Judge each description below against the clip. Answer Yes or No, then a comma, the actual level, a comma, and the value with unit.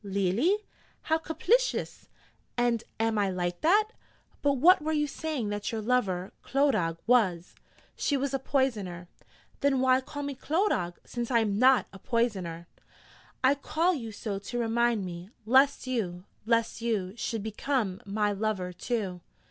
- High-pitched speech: Yes, high, 230 Hz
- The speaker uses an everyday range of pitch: No, wide, 5.7 semitones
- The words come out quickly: No, average, 150 wpm